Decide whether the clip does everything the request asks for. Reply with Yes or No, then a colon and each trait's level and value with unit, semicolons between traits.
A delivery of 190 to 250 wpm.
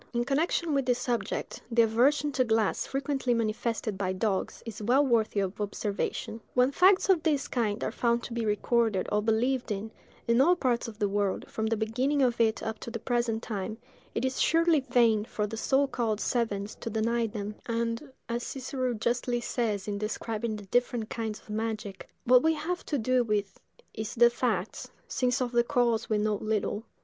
Yes: average, 195 wpm